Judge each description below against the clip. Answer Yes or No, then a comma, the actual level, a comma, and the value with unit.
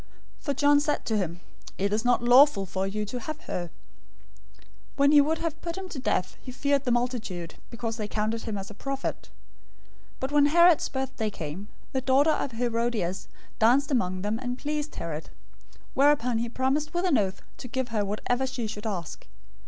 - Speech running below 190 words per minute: No, average, 200 wpm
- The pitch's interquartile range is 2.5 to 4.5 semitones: No, average, 5.1 semitones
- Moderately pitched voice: No, high, 245 Hz